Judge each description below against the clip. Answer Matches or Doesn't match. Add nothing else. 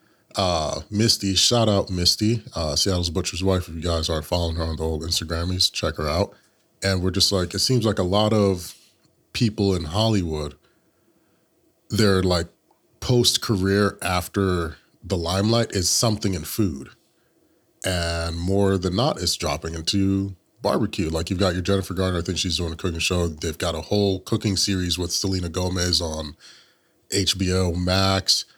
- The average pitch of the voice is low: Matches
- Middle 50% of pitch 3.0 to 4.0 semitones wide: Doesn't match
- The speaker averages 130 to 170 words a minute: Matches